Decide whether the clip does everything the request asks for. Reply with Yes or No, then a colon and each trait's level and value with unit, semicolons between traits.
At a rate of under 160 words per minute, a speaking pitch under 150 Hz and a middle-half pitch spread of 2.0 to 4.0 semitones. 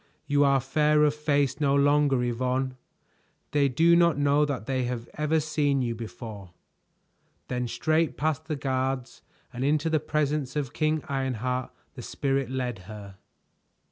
Yes: average, 150 wpm; medium, 140 Hz; average, 2.9 semitones